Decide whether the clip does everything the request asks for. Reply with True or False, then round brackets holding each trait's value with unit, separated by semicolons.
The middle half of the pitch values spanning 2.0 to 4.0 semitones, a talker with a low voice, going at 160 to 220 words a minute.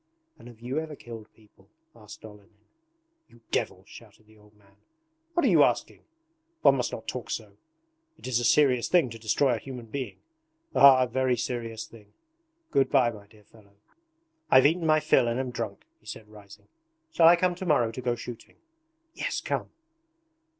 True (3.5 semitones; 120 Hz; 185 wpm)